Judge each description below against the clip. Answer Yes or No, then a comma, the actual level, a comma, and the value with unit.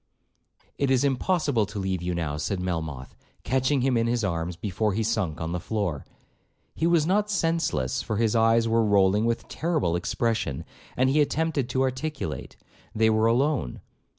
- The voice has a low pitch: Yes, low, 115 Hz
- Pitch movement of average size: No, wide, 6.6 semitones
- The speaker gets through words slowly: No, average, 170 wpm